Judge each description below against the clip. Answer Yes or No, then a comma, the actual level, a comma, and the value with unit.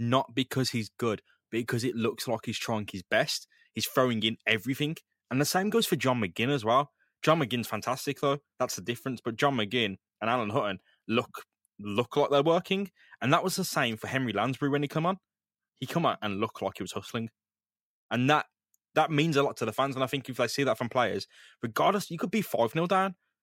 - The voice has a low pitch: Yes, low, 130 Hz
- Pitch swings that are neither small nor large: Yes, average, 4.4 semitones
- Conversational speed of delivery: No, fast, 230 wpm